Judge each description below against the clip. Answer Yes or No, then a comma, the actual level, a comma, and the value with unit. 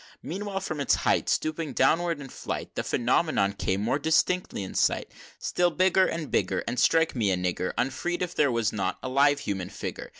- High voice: No, medium, 145 Hz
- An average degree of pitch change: No, wide, 6.7 semitones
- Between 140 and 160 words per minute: No, average, 200 wpm